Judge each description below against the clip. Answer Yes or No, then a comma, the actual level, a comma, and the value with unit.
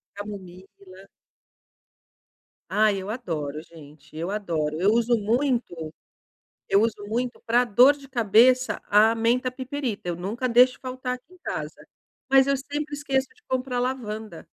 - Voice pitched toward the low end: No, high, 230 Hz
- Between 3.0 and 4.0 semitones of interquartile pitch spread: No, average, 4.6 semitones